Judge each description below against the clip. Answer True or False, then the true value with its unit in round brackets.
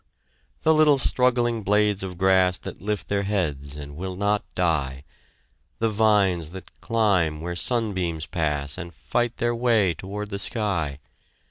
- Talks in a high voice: False (95 Hz)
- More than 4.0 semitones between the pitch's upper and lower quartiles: True (4.5 semitones)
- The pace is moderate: True (145 wpm)